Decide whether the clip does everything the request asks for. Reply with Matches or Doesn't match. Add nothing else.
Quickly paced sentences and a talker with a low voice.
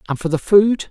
Doesn't match